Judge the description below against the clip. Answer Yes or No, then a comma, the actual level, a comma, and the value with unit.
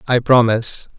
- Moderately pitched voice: No, low, 115 Hz